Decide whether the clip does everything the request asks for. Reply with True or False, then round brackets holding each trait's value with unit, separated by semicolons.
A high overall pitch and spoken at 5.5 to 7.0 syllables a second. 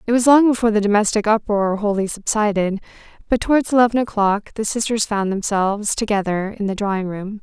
True (210 Hz; 5.9 syllables/s)